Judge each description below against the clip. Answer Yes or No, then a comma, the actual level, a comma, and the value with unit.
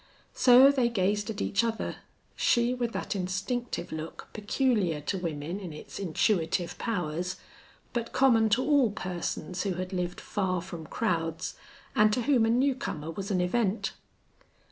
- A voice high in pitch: Yes, high, 200 Hz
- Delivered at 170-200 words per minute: No, average, 155 wpm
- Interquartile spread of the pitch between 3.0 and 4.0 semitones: No, average, 4.9 semitones